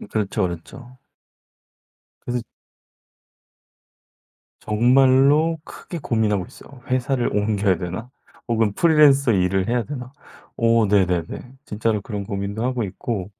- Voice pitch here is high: No, low, 115 Hz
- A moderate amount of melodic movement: Yes, average, 4.3 semitones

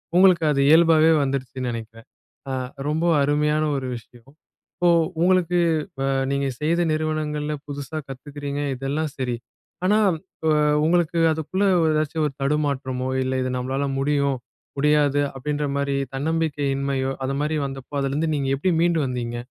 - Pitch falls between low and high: Yes, medium, 145 Hz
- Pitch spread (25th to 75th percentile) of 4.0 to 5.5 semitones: No, average, 2.7 semitones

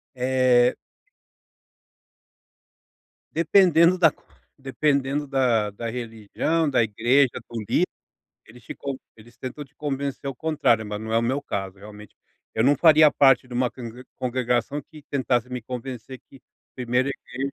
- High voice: No, low, 130 Hz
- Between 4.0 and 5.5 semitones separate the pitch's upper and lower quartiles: No, average, 3.2 semitones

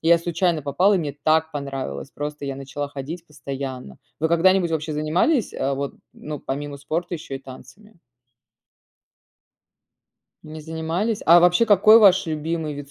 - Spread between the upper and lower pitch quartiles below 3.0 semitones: No, average, 3.6 semitones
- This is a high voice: No, medium, 155 Hz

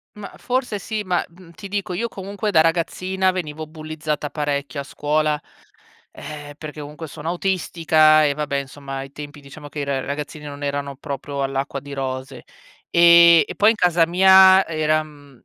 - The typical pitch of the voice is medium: Yes, medium, 155 Hz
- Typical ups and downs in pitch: Yes, average, 3.7 semitones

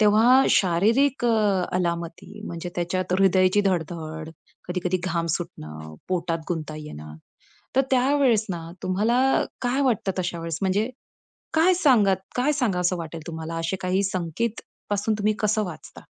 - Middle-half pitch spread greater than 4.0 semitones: Yes, average, 4.6 semitones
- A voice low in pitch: No, medium, 185 Hz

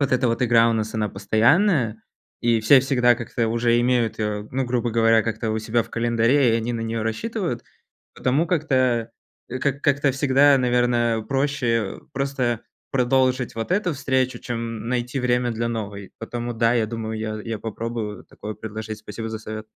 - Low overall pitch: Yes, low, 120 Hz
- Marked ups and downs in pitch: No, narrow, 2.5 semitones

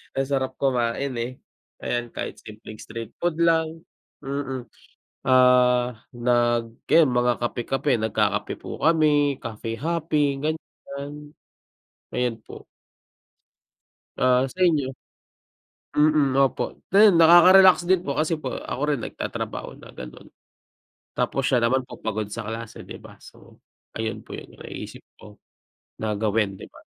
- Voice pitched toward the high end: No, low, 130 Hz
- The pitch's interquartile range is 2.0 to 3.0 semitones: No, average, 4.7 semitones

